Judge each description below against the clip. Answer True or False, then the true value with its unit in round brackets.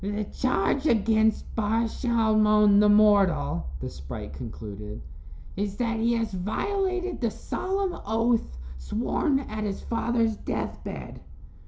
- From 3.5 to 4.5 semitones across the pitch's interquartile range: False (2.8 semitones)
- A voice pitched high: True (215 Hz)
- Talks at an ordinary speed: False (125 wpm)